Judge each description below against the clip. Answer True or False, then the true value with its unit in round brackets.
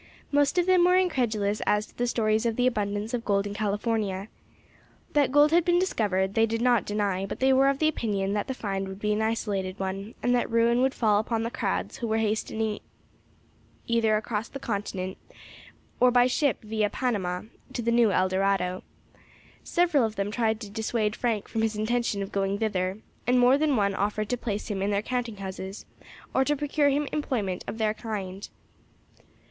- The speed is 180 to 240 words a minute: True (195 wpm)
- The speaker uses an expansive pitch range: False (3.5 semitones)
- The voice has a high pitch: True (220 Hz)